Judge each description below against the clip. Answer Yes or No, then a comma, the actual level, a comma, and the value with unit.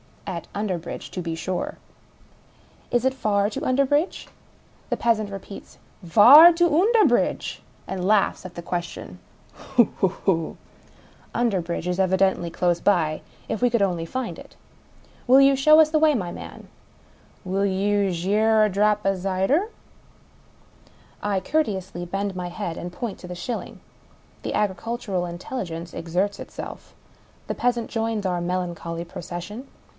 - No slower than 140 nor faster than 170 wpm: Yes, average, 165 wpm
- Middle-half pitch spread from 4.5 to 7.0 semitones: Yes, average, 4.8 semitones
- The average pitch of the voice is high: Yes, high, 195 Hz